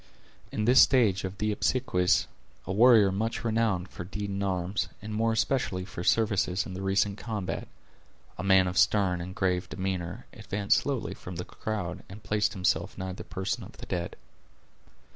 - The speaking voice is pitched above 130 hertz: No, low, 100 Hz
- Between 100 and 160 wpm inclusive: No, average, 175 wpm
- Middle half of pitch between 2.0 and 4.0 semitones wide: Yes, average, 2.7 semitones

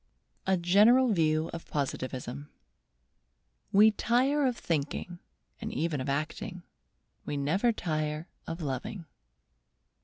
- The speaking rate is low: Yes, slow, 110 wpm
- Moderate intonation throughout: No, wide, 5.8 semitones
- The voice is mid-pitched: Yes, medium, 165 Hz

